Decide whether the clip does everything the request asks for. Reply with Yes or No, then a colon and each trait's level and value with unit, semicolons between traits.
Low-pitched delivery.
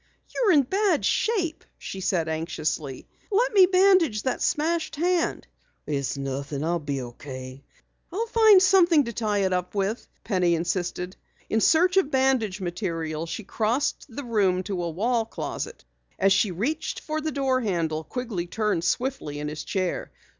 No: high, 210 Hz